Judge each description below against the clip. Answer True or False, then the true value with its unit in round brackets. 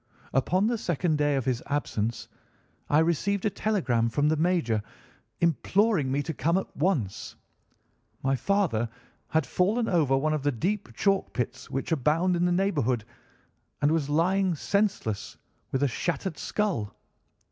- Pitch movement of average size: False (5.9 semitones)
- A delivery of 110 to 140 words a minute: False (150 wpm)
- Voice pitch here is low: False (160 Hz)